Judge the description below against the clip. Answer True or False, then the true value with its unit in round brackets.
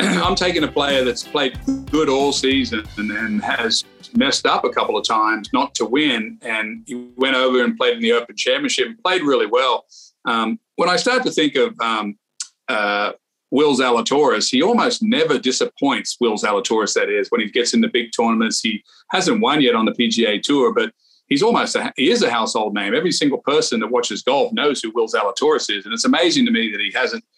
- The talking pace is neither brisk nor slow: False (215 wpm)